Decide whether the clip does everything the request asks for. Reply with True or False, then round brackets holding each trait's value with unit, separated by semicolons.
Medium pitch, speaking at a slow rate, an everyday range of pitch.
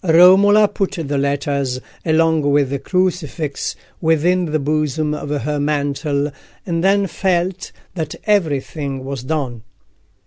True (155 Hz; 125 wpm; 4.0 semitones)